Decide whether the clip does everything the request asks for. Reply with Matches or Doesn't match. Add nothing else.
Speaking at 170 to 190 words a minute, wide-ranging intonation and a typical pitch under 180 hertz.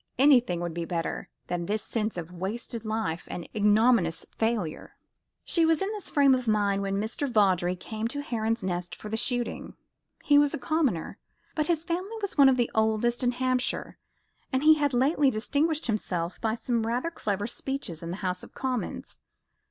Doesn't match